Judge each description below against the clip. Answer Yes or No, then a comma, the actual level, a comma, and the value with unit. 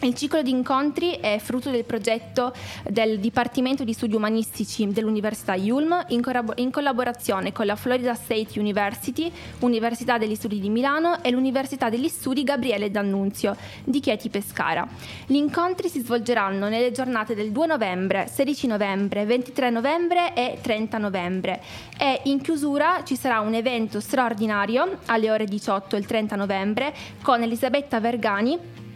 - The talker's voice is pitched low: No, high, 240 Hz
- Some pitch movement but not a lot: Yes, average, 4.0 semitones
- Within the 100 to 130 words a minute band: No, average, 145 wpm